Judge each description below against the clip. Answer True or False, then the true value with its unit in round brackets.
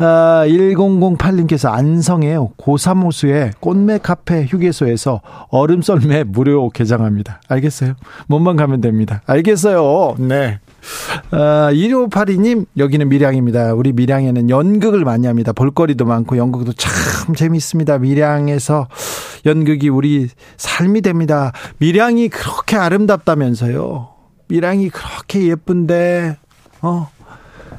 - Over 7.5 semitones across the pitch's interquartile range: False (5.1 semitones)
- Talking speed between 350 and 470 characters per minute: False (270 characters per minute)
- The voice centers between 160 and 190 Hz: False (150 Hz)